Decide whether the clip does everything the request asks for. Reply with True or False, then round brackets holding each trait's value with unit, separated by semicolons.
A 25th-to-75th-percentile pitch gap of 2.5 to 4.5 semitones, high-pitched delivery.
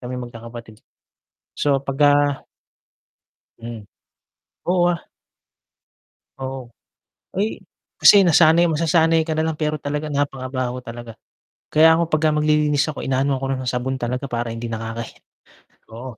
False (4.1 semitones; 135 Hz)